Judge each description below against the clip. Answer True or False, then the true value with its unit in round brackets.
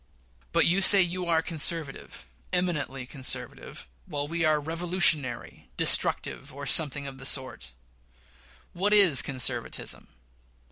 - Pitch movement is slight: False (4.5 semitones)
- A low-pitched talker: False (150 Hz)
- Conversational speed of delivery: False (120 wpm)